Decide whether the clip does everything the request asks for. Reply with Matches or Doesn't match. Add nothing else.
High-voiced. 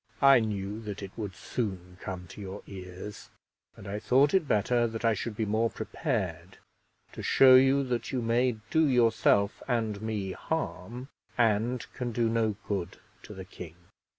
Doesn't match